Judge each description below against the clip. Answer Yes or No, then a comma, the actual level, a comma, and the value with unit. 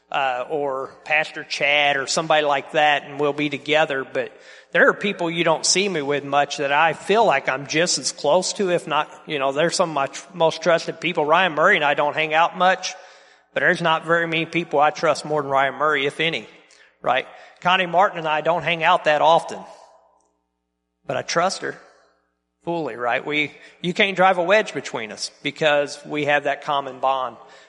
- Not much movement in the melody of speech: No, average, 3.1 semitones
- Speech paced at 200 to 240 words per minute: Yes, fast, 205 wpm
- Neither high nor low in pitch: Yes, medium, 155 Hz